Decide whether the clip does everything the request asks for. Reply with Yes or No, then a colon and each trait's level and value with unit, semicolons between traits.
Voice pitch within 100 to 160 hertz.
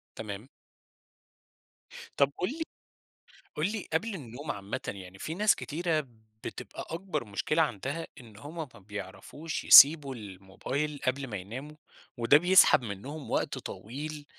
Yes: medium, 140 Hz